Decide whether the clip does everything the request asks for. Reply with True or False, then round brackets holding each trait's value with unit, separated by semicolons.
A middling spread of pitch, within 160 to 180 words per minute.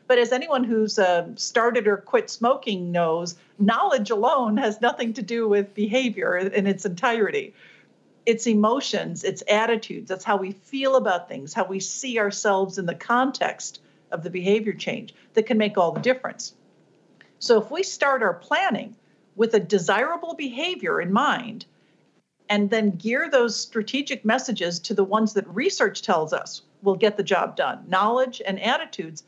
True (4.2 semitones; 165 wpm)